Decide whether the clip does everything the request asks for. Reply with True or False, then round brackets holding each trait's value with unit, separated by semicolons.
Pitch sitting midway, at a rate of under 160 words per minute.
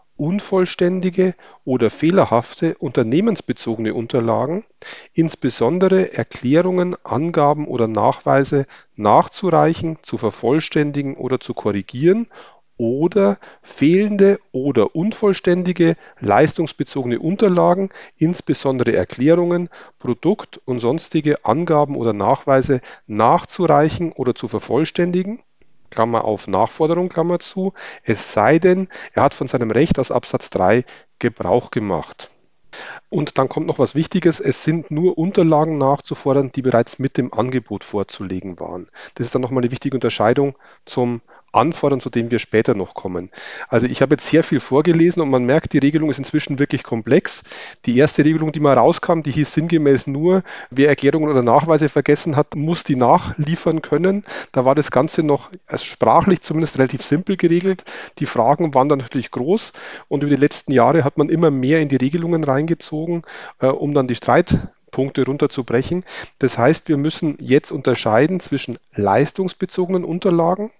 True (150 Hz; 140 wpm)